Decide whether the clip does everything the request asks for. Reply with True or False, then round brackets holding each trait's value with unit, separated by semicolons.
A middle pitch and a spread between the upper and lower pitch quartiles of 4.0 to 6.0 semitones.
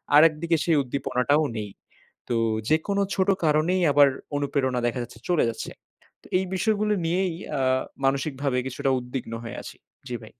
True (145 Hz; 5.3 semitones)